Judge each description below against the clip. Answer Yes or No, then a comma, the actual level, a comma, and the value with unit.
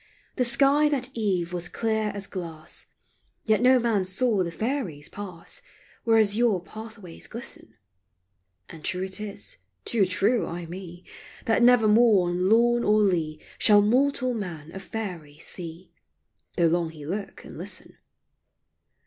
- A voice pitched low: No, high, 200 Hz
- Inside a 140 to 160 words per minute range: Yes, average, 150 wpm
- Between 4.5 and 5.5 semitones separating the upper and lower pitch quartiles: Yes, average, 4.8 semitones